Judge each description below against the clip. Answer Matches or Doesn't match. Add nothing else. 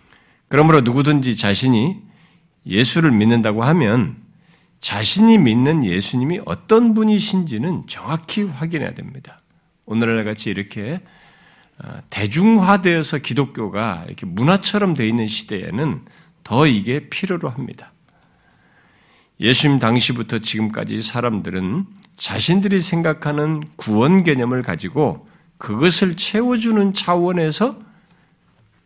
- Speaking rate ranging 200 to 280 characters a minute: Matches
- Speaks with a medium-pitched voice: Matches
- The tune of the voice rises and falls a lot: Matches